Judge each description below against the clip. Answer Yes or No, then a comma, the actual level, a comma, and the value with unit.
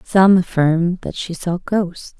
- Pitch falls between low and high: Yes, medium, 180 Hz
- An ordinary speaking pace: Yes, average, 165 wpm